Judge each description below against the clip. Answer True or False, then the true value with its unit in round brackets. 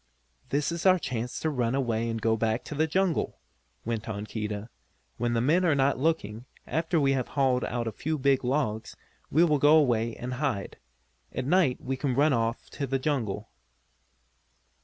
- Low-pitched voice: True (130 Hz)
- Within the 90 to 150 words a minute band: False (185 wpm)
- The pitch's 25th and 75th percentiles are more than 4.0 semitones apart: True (4.6 semitones)